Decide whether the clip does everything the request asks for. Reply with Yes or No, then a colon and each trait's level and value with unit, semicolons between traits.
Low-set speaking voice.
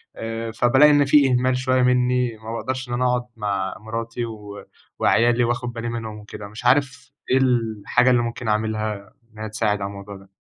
Yes: low, 115 Hz